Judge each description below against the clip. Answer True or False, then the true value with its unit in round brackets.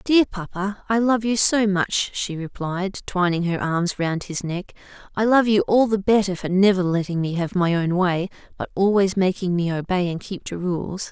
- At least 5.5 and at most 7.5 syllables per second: False (4.8 syllables/s)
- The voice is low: False (190 Hz)